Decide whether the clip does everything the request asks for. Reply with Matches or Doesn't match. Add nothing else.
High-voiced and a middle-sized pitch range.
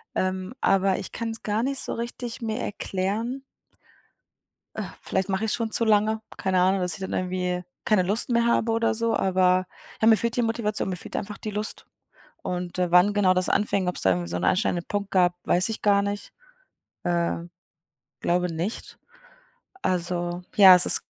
Matches